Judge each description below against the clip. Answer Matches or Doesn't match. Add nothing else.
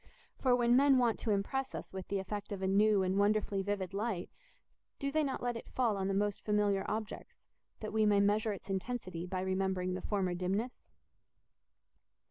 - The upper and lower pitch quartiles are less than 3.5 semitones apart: Matches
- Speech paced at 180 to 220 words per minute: Matches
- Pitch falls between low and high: Doesn't match